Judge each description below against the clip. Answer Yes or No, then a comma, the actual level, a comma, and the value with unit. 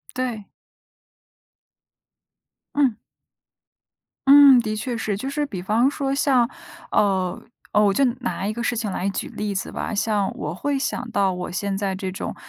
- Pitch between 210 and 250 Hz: Yes, high, 215 Hz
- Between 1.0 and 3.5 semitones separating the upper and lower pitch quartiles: No, average, 4.8 semitones